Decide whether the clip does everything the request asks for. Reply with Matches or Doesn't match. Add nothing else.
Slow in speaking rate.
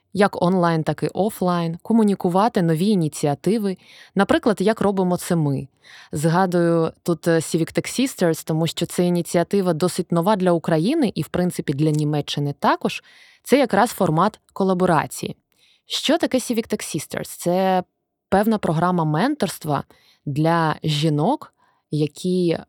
Doesn't match